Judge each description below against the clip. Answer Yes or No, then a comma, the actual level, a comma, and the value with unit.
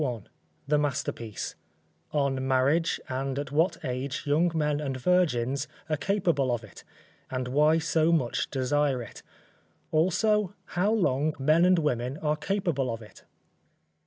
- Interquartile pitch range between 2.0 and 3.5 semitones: No, average, 4.0 semitones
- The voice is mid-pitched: Yes, medium, 145 Hz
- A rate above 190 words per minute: No, average, 145 wpm